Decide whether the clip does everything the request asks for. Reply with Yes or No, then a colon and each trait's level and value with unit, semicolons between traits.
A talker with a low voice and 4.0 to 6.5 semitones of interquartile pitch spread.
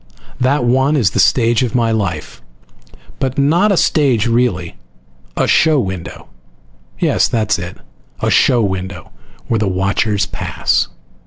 Yes: low, 115 Hz; average, 5.2 semitones